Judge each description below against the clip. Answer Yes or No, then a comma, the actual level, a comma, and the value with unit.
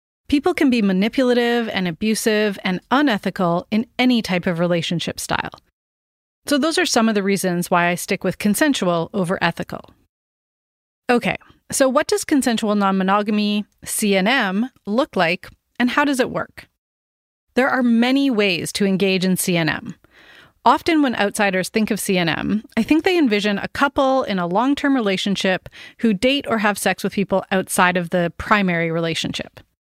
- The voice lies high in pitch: Yes, high, 205 Hz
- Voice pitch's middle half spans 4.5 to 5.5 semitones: Yes, average, 5.2 semitones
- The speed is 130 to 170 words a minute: Yes, average, 160 wpm